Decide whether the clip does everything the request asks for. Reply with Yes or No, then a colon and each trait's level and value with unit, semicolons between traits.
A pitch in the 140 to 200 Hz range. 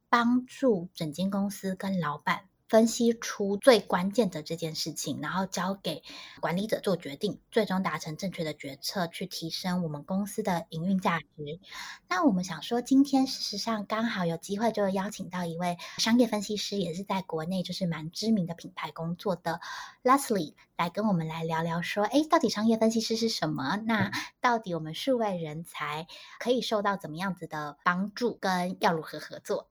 Yes: high, 190 Hz